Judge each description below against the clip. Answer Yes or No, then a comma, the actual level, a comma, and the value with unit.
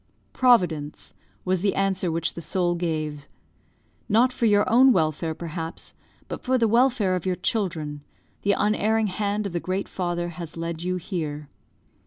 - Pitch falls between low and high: Yes, medium, 180 Hz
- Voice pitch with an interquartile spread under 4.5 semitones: Yes, average, 4.1 semitones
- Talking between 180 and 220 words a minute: No, average, 160 wpm